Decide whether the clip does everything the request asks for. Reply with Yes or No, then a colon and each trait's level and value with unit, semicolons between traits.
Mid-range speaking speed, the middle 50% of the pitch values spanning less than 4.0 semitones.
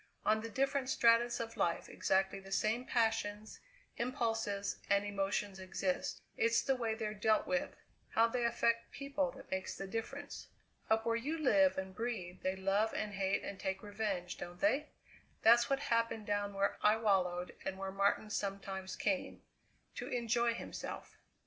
Yes: average, 160 wpm; average, 3.3 semitones